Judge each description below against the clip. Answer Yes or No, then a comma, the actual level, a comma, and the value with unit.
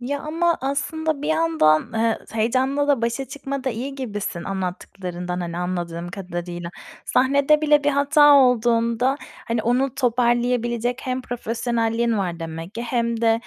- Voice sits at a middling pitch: No, high, 235 Hz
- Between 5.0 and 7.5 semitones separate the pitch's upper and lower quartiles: Yes, wide, 5.4 semitones